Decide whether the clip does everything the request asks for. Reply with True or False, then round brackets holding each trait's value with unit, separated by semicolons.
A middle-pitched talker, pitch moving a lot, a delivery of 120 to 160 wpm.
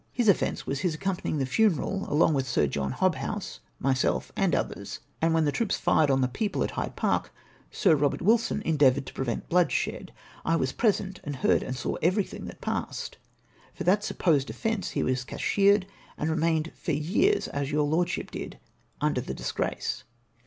False (160 Hz; 5.9 semitones; 180 wpm)